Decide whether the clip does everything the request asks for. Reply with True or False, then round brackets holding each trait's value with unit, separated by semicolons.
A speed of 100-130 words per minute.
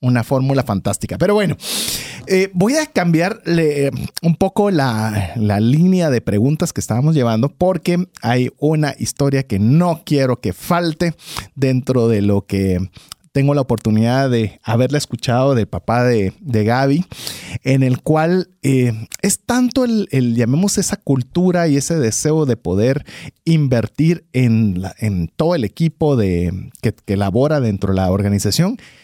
False (150 wpm)